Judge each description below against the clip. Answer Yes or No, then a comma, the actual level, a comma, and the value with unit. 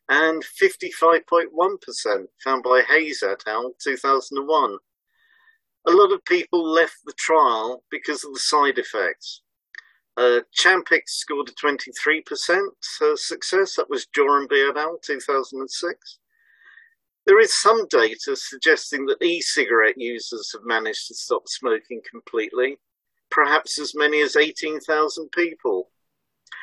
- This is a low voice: No, very high, 365 Hz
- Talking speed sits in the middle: No, slow, 115 wpm